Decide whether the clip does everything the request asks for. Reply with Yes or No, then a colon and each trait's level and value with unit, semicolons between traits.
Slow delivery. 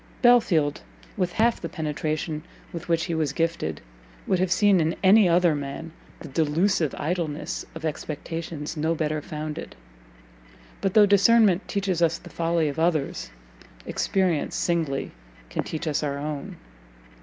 No: average, 145 wpm